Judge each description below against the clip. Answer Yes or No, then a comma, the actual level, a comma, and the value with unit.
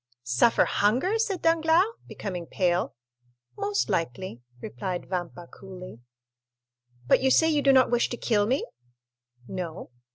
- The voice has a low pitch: No, high, 205 Hz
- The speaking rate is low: Yes, slow, 130 wpm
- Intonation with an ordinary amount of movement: No, wide, 8.9 semitones